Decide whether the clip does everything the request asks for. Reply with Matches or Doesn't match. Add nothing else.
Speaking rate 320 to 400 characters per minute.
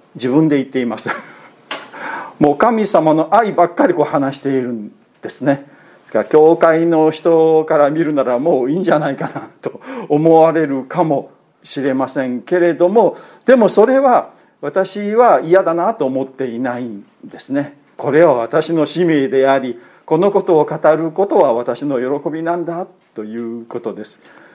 Doesn't match